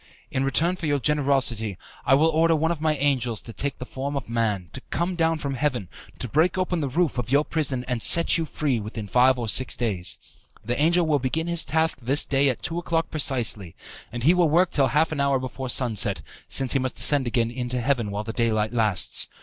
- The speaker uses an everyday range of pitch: Yes, average, 4.8 semitones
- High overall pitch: No, low, 135 Hz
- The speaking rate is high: Yes, fast, 225 wpm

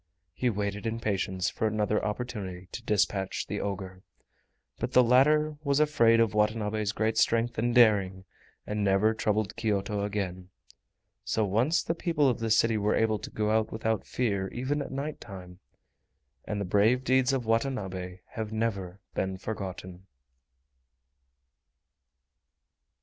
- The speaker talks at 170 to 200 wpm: No, average, 145 wpm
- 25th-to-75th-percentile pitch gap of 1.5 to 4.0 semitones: Yes, average, 3.3 semitones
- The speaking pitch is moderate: No, low, 110 Hz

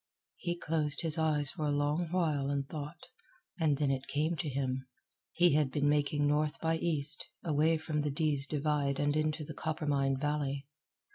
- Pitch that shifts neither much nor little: No, narrow, 1.8 semitones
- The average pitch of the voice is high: No, medium, 150 Hz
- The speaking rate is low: No, average, 180 wpm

